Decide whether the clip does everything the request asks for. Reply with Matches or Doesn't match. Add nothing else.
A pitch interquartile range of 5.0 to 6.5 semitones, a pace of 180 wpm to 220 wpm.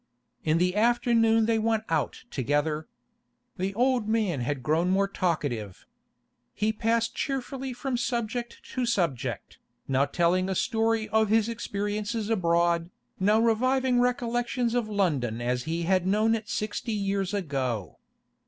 Doesn't match